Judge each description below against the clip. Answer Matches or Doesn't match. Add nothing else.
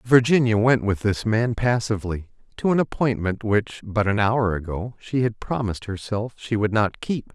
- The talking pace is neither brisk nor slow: Matches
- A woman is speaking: Doesn't match